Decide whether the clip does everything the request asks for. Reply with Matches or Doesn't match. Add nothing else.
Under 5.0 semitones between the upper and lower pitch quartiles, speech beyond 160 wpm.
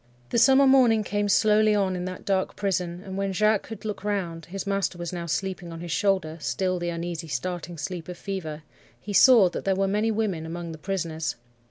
Matches